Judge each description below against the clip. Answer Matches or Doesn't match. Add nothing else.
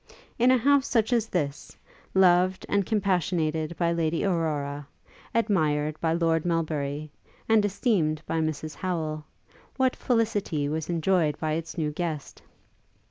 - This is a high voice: Doesn't match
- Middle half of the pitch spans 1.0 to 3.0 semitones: Doesn't match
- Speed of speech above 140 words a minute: Doesn't match